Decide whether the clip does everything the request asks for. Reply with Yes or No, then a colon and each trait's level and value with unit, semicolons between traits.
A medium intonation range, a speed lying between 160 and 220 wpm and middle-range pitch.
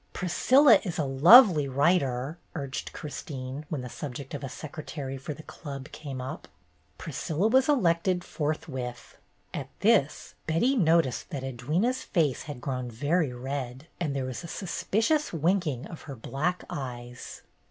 No: average, 4.8 semitones; average, 150 wpm; medium, 150 Hz